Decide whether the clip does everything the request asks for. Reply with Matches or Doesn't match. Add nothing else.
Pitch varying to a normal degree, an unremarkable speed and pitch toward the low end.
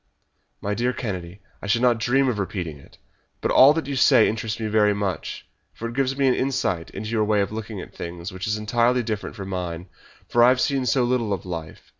Doesn't match